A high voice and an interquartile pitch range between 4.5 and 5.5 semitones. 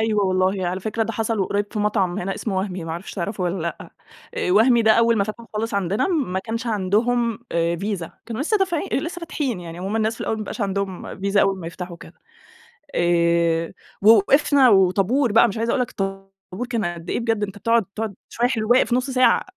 No: high, 205 Hz; average, 3.7 semitones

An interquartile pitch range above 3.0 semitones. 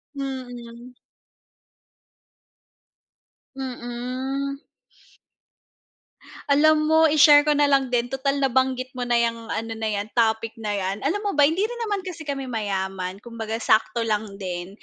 Yes: average, 4.0 semitones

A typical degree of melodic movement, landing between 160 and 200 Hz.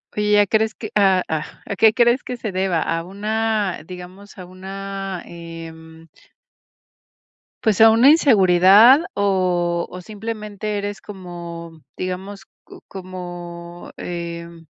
Yes: average, 3.3 semitones; high, 190 Hz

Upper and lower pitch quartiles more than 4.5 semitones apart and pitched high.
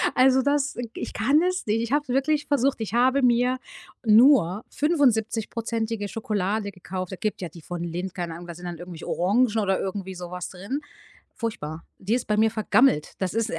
Yes: wide, 5.6 semitones; high, 215 Hz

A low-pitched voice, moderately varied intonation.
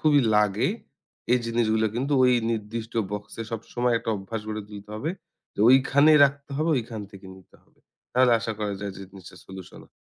Yes: low, 115 Hz; average, 3.6 semitones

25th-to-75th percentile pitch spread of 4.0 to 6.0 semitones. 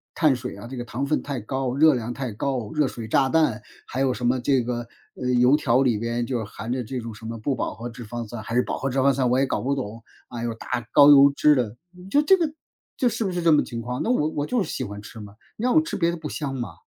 No: average, 3.5 semitones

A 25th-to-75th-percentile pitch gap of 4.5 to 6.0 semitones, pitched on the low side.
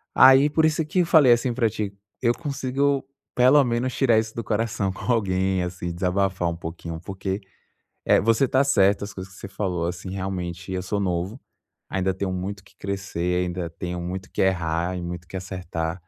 Yes: average, 4.8 semitones; very low, 95 Hz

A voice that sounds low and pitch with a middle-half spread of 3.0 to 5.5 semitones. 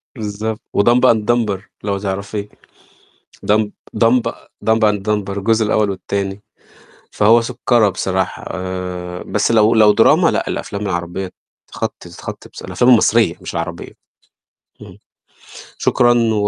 No: low, 105 Hz; narrow, 2.5 semitones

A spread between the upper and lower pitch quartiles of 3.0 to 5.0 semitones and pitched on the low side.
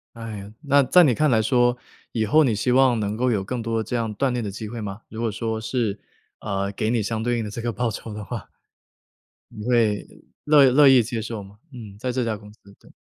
No: narrow, 2.6 semitones; low, 115 Hz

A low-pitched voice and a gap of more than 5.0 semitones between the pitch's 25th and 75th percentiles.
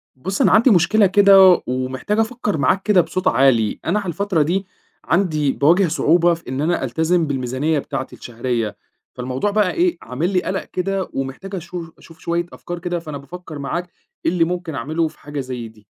No: medium, 170 Hz; wide, 5.6 semitones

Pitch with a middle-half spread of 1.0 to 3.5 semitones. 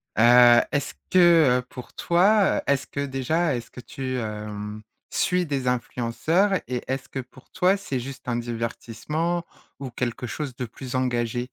No: average, 4.6 semitones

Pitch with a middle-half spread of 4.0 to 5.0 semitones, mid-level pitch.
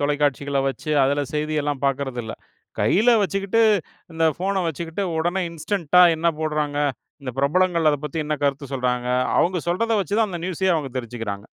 Yes: average, 4.4 semitones; medium, 155 Hz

